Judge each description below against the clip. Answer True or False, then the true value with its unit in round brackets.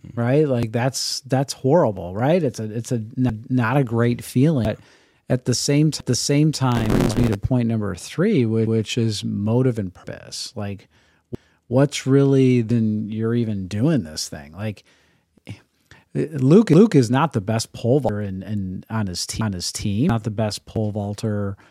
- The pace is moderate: True (170 wpm)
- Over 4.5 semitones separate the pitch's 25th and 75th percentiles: False (3.4 semitones)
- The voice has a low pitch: True (115 Hz)